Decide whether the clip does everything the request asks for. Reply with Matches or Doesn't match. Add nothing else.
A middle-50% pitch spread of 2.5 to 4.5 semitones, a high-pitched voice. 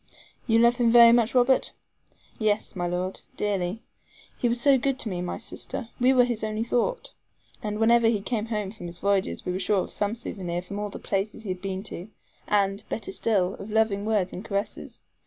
Matches